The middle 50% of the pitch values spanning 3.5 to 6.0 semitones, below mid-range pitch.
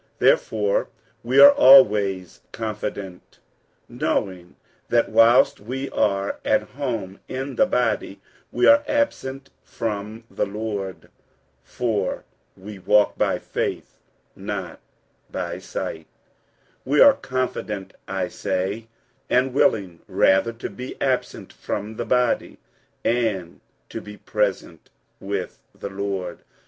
Yes: average, 4.6 semitones; low, 105 Hz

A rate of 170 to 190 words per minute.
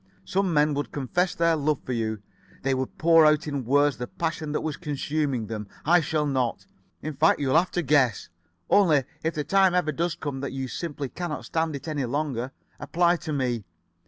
No: average, 200 wpm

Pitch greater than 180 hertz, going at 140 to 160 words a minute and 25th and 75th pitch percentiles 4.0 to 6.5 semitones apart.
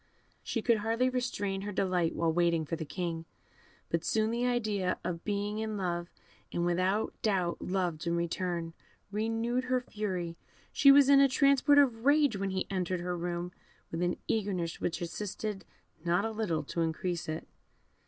No: high, 190 Hz; average, 175 wpm; average, 4.6 semitones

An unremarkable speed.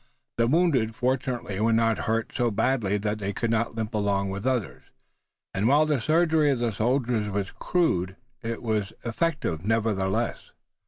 Yes: average, 165 wpm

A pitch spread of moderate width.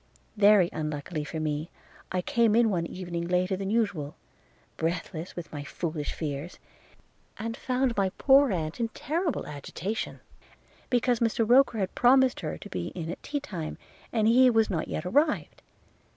No: wide, 6.5 semitones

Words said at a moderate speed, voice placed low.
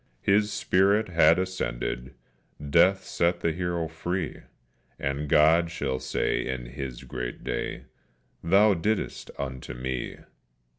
No: slow, 120 wpm; very low, 80 Hz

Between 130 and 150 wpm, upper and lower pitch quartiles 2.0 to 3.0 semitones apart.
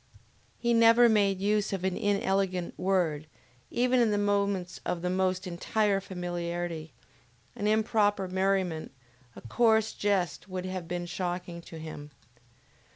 Yes: slow, 135 wpm; average, 2.7 semitones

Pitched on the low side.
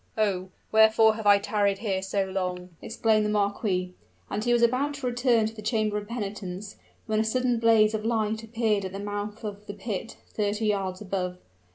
No: high, 210 Hz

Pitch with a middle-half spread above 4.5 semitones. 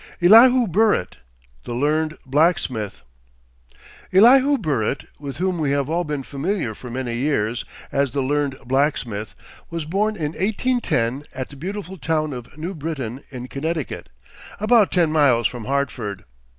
Yes: wide, 5.6 semitones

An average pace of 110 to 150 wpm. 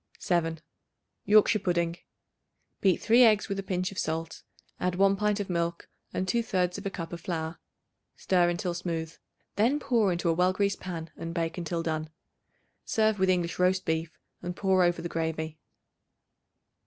No: average, 165 wpm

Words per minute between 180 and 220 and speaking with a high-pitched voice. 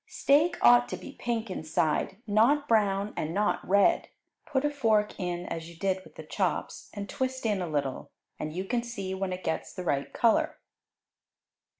Yes: average, 185 wpm; high, 200 Hz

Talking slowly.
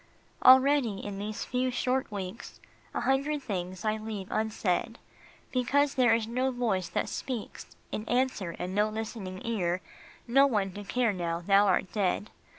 No: average, 155 wpm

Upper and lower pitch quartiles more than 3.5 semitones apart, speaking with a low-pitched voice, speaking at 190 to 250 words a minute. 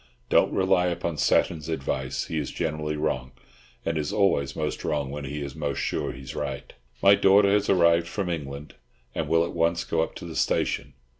No: average, 3.1 semitones; very low, 80 Hz; average, 200 wpm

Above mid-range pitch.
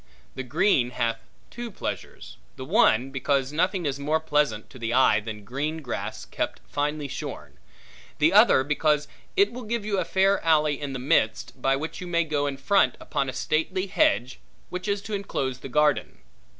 No: medium, 150 Hz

